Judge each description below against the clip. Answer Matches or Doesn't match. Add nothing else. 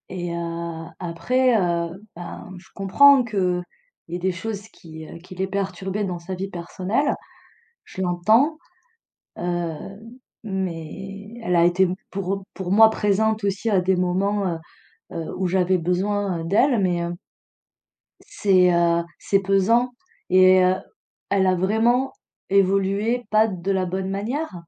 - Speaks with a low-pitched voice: Doesn't match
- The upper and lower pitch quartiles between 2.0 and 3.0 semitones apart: Matches